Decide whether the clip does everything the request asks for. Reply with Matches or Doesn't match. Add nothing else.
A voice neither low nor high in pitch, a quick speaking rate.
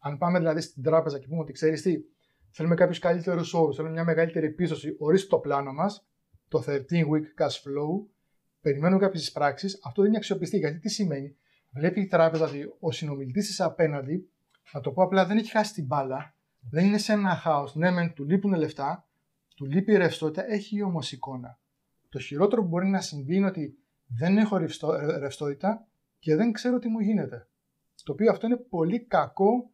Matches